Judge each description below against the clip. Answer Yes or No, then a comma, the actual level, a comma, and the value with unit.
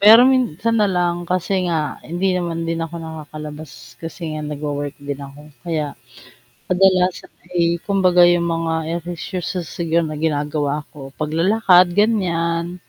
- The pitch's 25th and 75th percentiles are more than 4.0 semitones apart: No, average, 3.0 semitones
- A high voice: No, medium, 170 Hz